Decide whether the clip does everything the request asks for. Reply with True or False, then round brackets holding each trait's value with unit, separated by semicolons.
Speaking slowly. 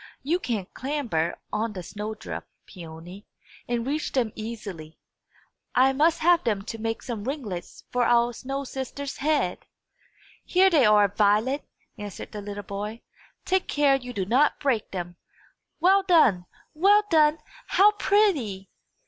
False (145 wpm)